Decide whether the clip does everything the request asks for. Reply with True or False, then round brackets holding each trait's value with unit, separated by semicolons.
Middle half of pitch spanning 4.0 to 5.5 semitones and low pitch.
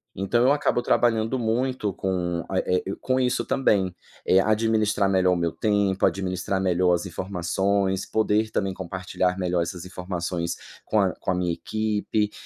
False (3.0 semitones; 95 Hz)